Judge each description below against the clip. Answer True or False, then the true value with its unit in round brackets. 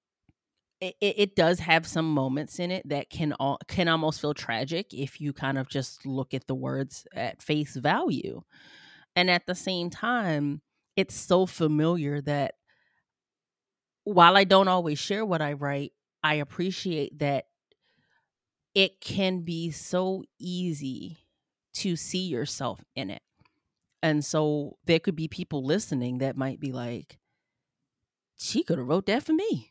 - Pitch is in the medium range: True (160 Hz)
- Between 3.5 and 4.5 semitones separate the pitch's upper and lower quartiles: True (4.2 semitones)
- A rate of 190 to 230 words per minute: False (150 wpm)